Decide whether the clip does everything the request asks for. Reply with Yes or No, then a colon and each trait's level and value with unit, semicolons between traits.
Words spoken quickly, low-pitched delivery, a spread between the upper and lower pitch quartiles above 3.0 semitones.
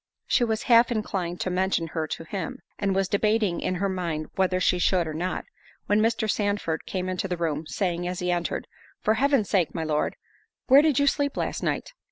No: fast, 210 wpm; medium, 185 Hz; average, 3.8 semitones